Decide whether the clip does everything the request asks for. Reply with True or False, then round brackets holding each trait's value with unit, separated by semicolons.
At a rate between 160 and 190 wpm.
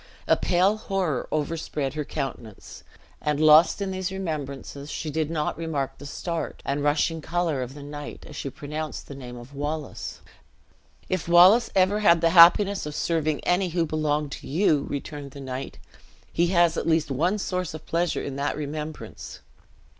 True (170 wpm)